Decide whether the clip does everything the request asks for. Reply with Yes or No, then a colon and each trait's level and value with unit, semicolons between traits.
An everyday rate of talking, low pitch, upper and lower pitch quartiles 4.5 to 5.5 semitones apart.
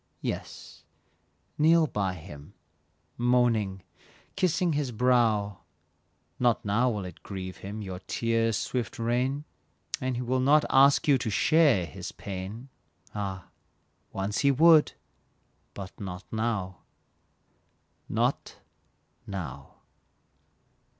No: slow, 105 wpm; low, 115 Hz; average, 5.1 semitones